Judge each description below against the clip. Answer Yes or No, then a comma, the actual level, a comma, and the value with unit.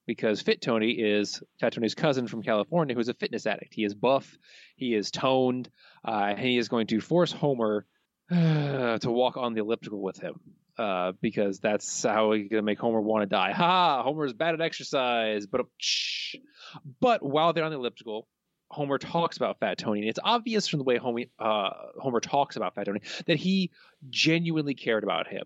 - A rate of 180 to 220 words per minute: Yes, average, 195 wpm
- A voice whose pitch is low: Yes, low, 125 Hz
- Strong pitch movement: Yes, wide, 6.0 semitones